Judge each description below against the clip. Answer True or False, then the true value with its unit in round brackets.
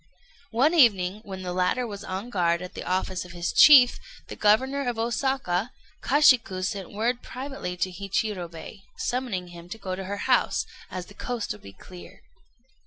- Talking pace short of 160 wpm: False (175 wpm)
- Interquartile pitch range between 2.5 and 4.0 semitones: False (5.1 semitones)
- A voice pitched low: False (200 Hz)